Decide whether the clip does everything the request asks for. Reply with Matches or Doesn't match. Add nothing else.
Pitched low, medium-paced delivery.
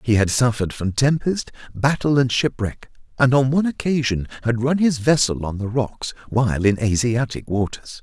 Matches